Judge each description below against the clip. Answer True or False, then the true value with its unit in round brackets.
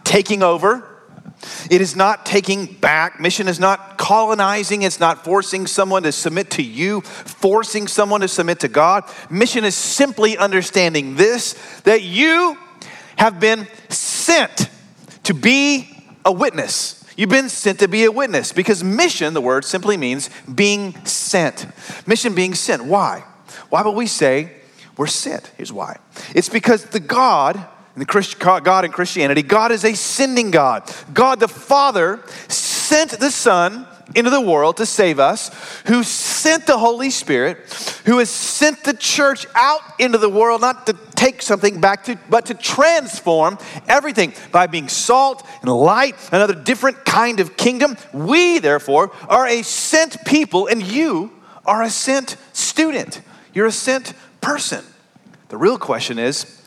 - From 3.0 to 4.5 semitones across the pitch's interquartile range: False (4.9 semitones)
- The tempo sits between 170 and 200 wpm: False (155 wpm)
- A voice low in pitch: False (215 Hz)